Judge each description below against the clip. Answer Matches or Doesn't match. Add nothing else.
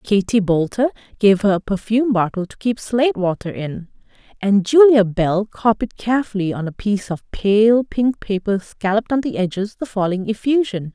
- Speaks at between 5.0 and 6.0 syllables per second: Matches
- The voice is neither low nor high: Doesn't match